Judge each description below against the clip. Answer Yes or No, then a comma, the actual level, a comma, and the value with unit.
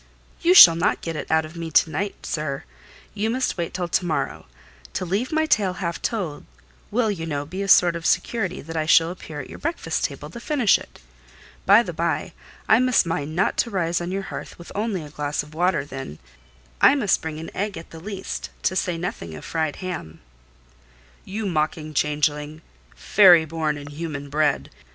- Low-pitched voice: No, medium, 170 Hz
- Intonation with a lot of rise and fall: No, average, 4.3 semitones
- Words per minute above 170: Yes, average, 195 wpm